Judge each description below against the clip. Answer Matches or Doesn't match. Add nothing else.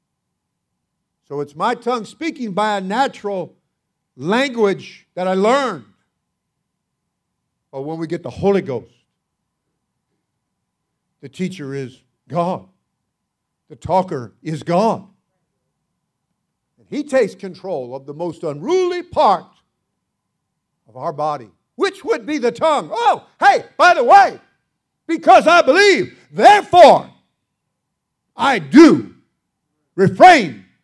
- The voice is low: Doesn't match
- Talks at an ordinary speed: Doesn't match